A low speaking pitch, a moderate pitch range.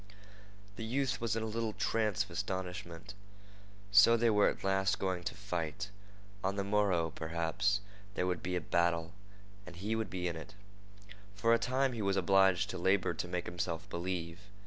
Yes: very low, 95 Hz; average, 3.1 semitones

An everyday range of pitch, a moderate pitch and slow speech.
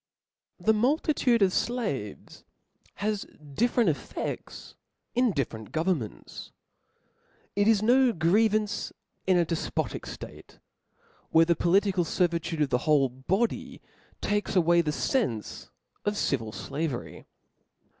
No: wide, 6.0 semitones; medium, 180 Hz; slow, 115 wpm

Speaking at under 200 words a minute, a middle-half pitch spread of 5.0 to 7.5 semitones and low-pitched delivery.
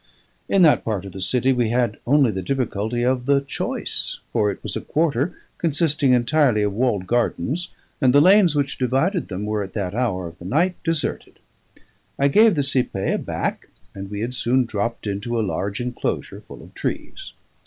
Yes: average, 190 wpm; wide, 5.5 semitones; low, 125 Hz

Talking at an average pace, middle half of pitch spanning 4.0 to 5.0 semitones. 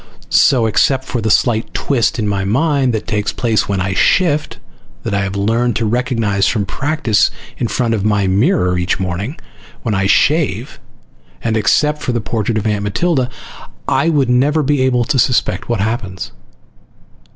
Yes: average, 175 wpm; average, 4.4 semitones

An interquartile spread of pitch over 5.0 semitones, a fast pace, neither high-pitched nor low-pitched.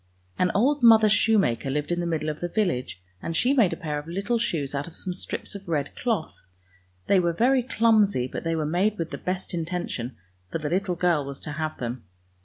Yes: wide, 5.5 semitones; fast, 220 wpm; medium, 175 Hz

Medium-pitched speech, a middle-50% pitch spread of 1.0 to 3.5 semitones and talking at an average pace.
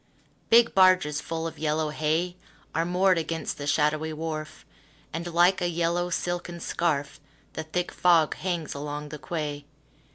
Yes: medium, 165 Hz; narrow, 2.5 semitones; average, 150 wpm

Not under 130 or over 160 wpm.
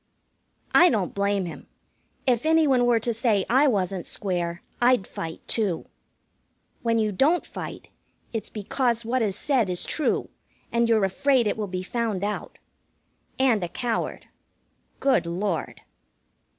Yes: average, 145 wpm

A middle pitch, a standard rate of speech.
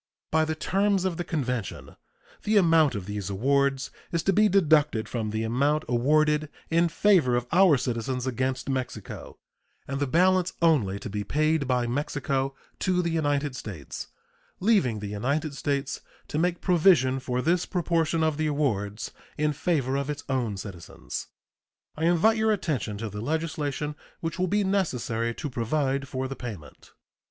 Yes: medium, 145 Hz; average, 165 wpm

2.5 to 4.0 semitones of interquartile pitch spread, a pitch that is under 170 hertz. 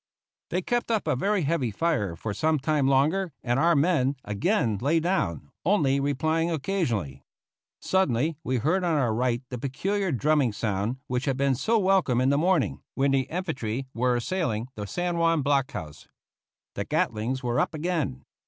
No: wide, 5.6 semitones; medium, 140 Hz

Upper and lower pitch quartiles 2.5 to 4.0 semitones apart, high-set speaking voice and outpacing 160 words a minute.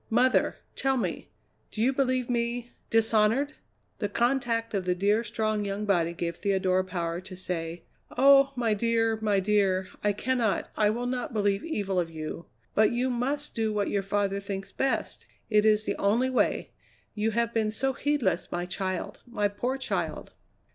Yes: average, 3.6 semitones; high, 215 Hz; average, 170 wpm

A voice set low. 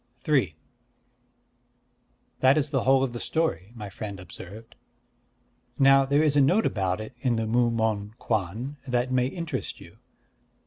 Yes: low, 120 Hz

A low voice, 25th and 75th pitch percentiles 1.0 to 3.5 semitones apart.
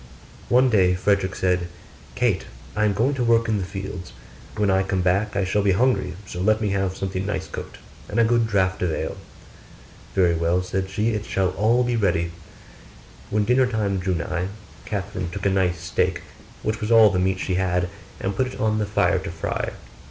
Yes: very low, 95 Hz; average, 2.7 semitones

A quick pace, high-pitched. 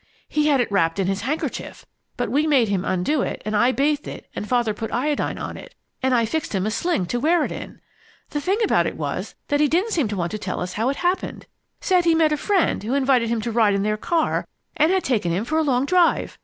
Yes: fast, 255 wpm; very high, 260 Hz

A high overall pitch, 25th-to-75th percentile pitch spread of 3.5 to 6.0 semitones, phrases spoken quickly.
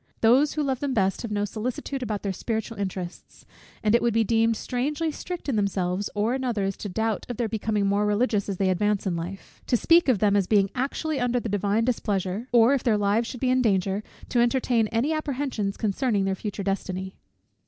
Yes: high, 220 Hz; average, 3.8 semitones; fast, 215 wpm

